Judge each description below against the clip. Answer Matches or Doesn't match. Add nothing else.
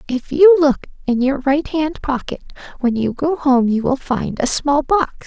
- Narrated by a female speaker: Matches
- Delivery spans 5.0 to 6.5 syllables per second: Doesn't match